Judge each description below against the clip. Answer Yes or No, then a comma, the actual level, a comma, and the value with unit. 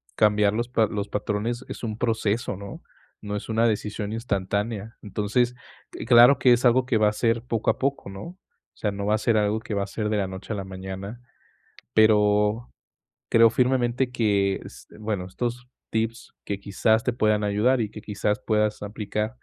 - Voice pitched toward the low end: Yes, low, 110 Hz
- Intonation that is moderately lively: No, narrow, 2.3 semitones